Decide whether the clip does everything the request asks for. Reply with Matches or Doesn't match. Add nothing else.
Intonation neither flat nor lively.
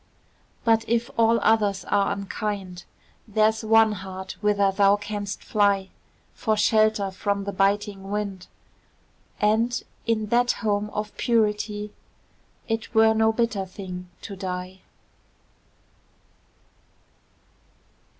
Doesn't match